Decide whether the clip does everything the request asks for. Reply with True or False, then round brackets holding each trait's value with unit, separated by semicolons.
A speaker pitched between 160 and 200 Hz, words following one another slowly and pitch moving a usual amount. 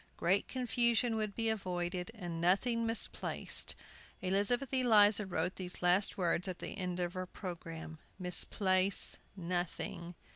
True (185 Hz; 125 wpm; 3.7 semitones)